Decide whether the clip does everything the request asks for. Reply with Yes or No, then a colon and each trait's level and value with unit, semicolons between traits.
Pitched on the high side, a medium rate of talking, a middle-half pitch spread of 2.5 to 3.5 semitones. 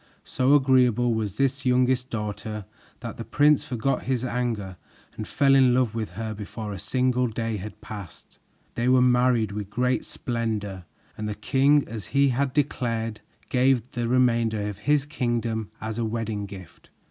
No: low, 120 Hz; average, 170 wpm; average, 3.0 semitones